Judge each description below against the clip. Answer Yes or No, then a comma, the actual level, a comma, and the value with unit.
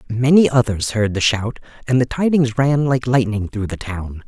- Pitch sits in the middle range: No, low, 120 Hz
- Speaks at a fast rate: No, average, 195 wpm